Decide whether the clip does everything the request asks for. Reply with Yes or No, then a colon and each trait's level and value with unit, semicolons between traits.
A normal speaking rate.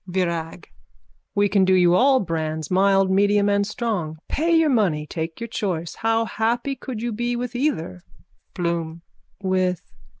Yes: average, 155 wpm